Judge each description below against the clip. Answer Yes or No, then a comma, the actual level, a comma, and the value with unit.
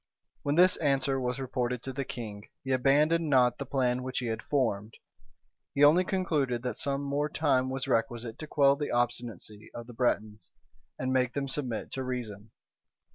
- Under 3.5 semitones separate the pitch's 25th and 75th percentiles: Yes, average, 2.7 semitones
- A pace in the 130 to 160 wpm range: No, average, 180 wpm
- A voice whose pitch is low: Yes, low, 130 Hz